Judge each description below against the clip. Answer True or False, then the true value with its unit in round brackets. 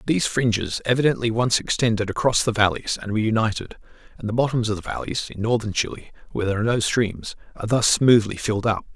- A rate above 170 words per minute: True (200 wpm)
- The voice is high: False (110 Hz)